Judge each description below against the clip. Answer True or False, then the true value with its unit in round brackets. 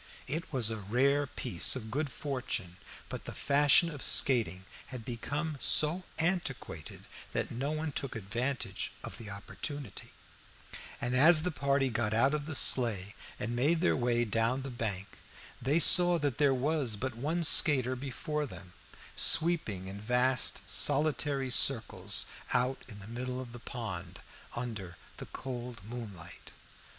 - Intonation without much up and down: False (4.3 semitones)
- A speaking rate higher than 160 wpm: False (150 wpm)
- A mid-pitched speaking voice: False (125 Hz)